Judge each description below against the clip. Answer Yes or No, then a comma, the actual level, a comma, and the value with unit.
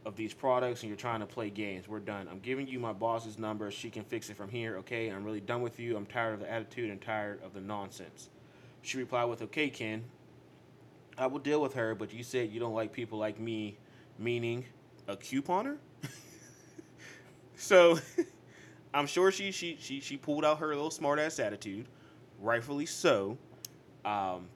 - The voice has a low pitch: Yes, low, 115 Hz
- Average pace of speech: Yes, average, 190 wpm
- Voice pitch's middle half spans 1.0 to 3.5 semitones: No, average, 4.2 semitones